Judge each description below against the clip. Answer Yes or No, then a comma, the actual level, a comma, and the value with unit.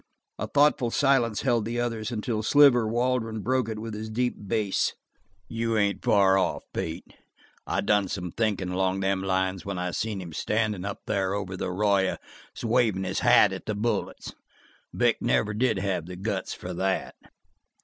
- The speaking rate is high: No, average, 170 wpm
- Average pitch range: Yes, average, 3.2 semitones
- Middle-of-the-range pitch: No, low, 105 Hz